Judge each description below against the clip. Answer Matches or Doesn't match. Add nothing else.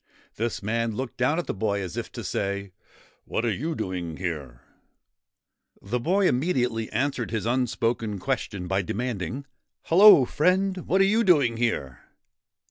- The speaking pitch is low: Matches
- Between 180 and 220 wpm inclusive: Doesn't match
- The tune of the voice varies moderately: Doesn't match